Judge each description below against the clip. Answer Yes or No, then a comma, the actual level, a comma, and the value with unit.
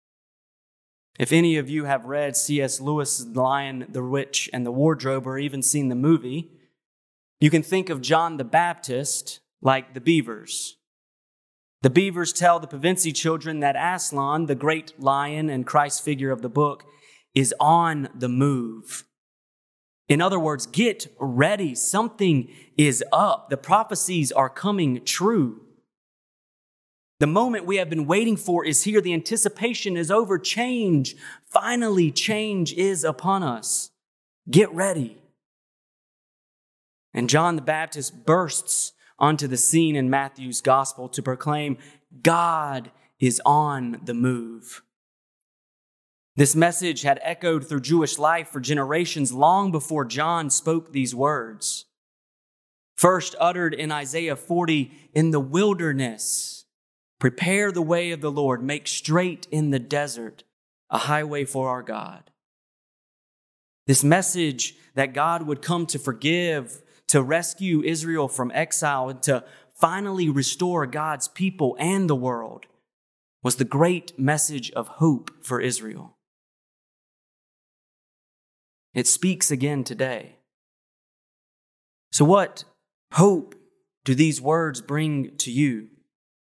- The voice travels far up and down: No, average, 4.0 semitones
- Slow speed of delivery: Yes, slow, 130 wpm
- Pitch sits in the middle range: Yes, medium, 150 Hz